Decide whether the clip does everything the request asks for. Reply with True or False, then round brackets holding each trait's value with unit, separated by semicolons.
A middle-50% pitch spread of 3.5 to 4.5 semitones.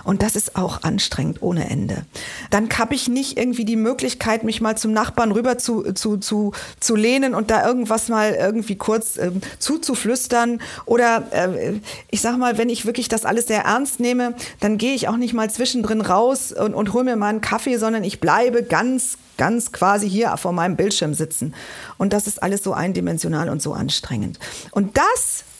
False (2.7 semitones)